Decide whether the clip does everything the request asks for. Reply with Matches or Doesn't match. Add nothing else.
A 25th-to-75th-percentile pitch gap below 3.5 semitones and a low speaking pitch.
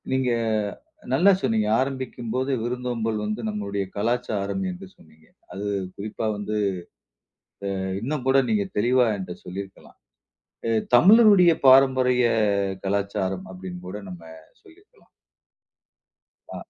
Doesn't match